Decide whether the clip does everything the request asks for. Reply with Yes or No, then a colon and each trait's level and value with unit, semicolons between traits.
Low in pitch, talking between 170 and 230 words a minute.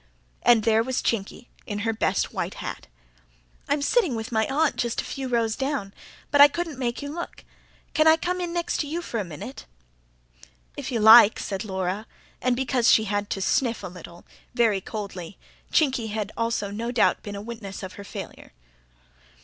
No: high, 230 Hz; average, 190 wpm